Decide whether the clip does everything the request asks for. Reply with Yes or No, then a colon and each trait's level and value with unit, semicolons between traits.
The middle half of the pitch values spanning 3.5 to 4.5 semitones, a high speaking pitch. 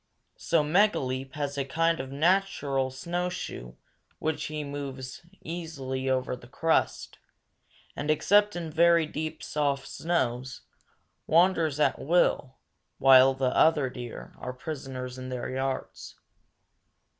No: average, 3.9 semitones; medium, 140 Hz